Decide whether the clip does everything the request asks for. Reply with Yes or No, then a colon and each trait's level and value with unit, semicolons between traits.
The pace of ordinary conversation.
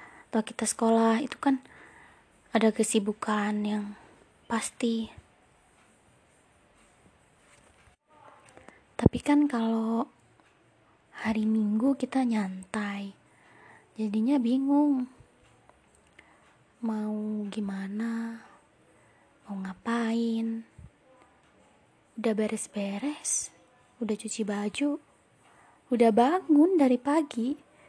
No: slow, 65 wpm